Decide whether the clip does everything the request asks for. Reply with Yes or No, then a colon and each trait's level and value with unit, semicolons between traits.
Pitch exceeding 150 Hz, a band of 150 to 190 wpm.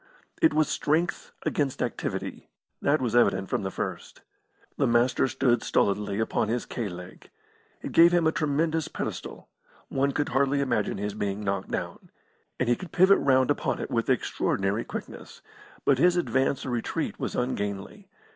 No: low, 130 Hz; average, 165 wpm